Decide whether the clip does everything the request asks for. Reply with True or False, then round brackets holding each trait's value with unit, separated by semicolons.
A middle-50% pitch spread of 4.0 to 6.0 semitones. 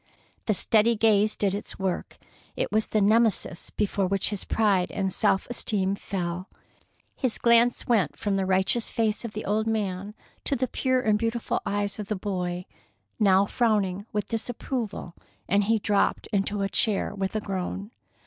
False (2.4 semitones)